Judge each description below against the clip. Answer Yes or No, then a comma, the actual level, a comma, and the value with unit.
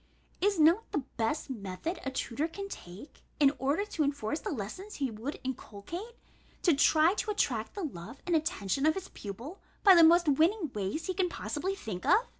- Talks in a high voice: Yes, very high, 305 Hz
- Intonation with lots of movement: Yes, wide, 7.6 semitones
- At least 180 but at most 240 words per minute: Yes, average, 190 wpm